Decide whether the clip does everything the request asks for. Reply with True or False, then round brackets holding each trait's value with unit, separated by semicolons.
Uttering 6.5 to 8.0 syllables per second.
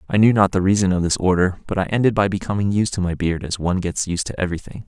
True (6.9 syllables/s)